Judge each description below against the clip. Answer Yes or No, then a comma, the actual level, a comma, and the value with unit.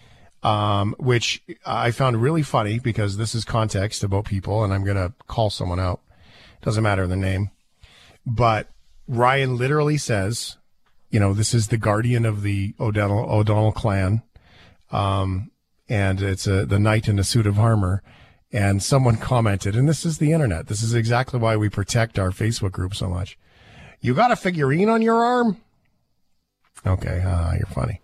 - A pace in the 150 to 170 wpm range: Yes, average, 165 wpm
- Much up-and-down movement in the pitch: No, average, 3.4 semitones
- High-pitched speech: No, low, 110 Hz